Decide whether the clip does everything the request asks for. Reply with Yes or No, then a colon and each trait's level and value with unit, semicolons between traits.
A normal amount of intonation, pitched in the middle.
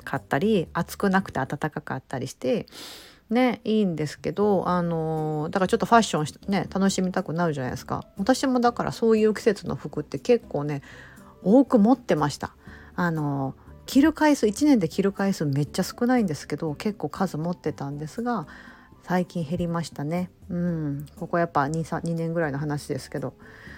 No: wide, 6.0 semitones; medium, 175 Hz